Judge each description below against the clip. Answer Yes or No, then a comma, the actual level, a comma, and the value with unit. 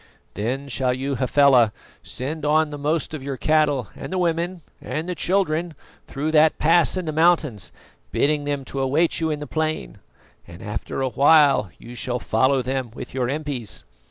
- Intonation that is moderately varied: Yes, average, 3.3 semitones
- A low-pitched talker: No, medium, 145 Hz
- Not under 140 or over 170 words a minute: No, average, 180 wpm